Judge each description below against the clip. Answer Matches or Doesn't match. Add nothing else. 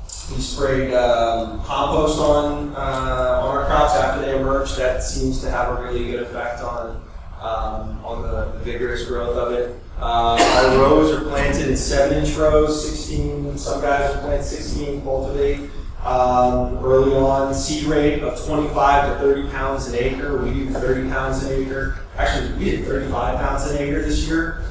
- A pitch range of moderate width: Matches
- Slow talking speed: Doesn't match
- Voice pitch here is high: Doesn't match